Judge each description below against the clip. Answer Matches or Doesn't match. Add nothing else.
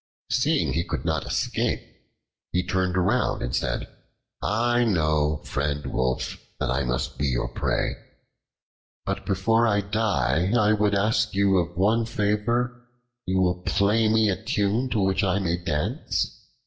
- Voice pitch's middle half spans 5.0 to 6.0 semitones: Doesn't match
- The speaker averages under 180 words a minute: Matches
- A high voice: Doesn't match